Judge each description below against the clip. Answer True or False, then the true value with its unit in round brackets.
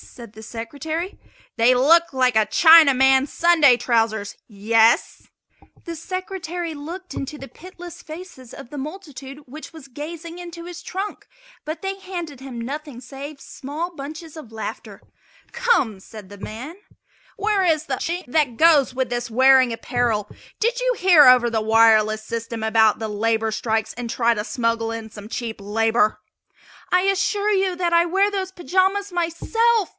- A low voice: False (275 Hz)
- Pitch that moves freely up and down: True (7.1 semitones)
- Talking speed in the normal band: True (160 wpm)